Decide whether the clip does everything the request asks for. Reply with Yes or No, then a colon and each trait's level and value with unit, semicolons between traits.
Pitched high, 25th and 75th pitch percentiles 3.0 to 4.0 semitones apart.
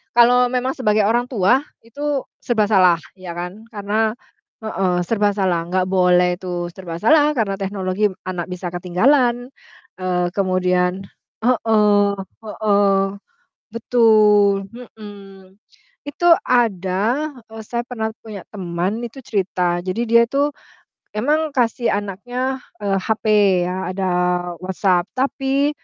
No: high, 205 Hz; average, 4.5 semitones